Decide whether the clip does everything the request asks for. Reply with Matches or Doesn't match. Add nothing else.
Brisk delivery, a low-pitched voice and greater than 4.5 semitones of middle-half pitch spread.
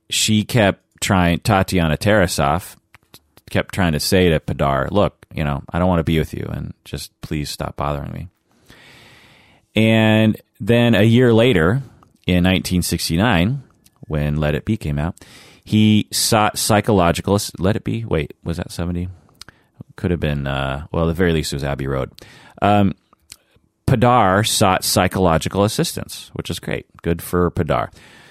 Doesn't match